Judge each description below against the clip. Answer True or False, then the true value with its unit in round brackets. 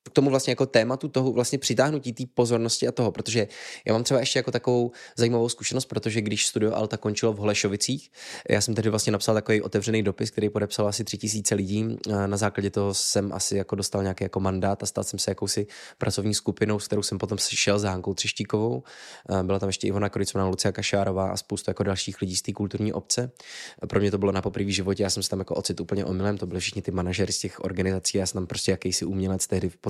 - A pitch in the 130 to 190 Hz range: False (105 Hz)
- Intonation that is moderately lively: False (2.3 semitones)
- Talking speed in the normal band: False (230 wpm)